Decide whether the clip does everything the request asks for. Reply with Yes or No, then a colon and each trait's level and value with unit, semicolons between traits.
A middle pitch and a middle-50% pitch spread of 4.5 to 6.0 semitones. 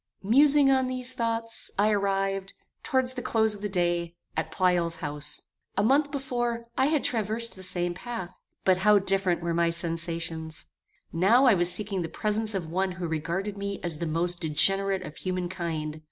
No: high, 195 Hz; average, 4.8 semitones